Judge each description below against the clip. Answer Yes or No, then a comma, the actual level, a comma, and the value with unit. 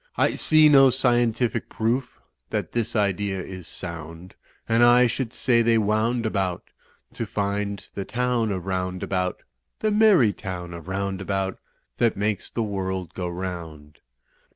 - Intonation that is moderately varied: Yes, average, 4.3 semitones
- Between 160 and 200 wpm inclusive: No, average, 140 wpm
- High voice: No, low, 100 Hz